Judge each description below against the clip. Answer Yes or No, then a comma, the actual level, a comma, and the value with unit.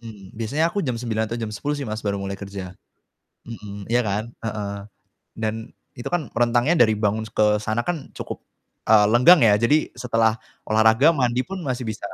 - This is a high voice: No, low, 115 Hz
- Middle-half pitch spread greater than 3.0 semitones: No, narrow, 2.5 semitones